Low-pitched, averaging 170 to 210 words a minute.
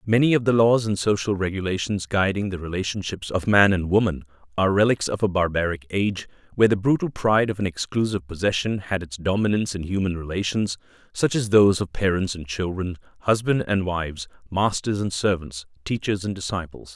Yes: very low, 95 Hz; average, 175 wpm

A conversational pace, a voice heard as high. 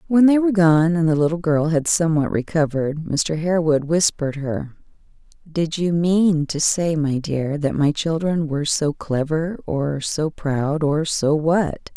No: average, 165 wpm; medium, 160 Hz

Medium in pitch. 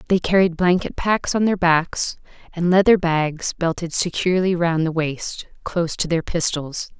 Yes: medium, 170 Hz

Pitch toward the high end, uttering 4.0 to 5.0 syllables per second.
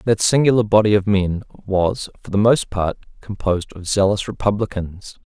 No: low, 100 Hz; 4.9 syllables/s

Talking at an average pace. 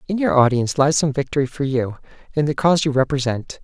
No: fast, 215 wpm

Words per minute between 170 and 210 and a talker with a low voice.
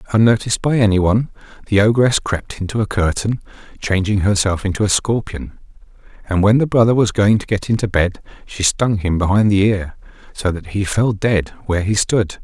Yes: average, 185 wpm; low, 105 Hz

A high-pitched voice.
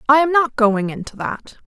Yes: very high, 250 Hz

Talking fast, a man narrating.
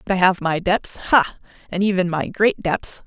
No: fast, 215 wpm; female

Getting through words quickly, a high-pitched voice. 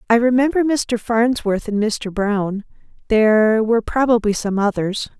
No: average, 140 wpm; high, 225 Hz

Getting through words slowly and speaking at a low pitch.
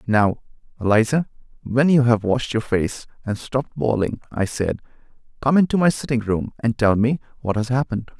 No: average, 175 wpm; low, 120 Hz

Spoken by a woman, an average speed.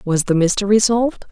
Yes: female; average, 180 wpm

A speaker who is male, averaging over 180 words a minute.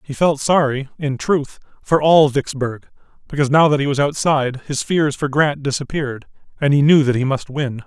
Yes: male; average, 200 wpm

